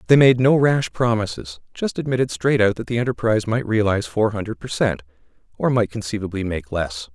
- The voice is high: No, low, 110 Hz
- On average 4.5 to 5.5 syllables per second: No, 5.8 syllables/s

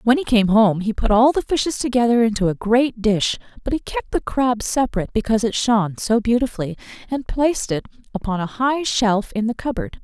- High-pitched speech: Yes, high, 230 Hz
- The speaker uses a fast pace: Yes, fast, 210 wpm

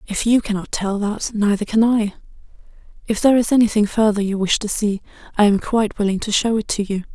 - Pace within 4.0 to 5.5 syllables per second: No, 6.0 syllables/s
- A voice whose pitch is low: No, high, 210 Hz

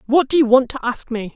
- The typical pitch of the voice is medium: No, very high, 250 Hz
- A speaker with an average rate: No, fast, 310 wpm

